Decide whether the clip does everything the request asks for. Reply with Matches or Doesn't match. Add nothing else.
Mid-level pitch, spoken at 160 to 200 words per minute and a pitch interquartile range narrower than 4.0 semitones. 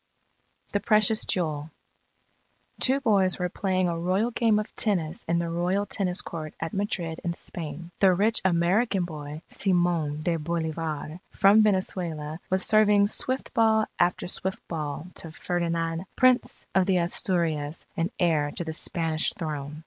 Doesn't match